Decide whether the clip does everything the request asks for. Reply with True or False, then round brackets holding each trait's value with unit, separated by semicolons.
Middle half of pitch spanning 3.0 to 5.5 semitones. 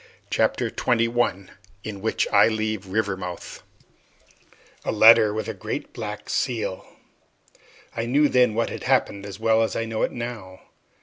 False (2.5 semitones)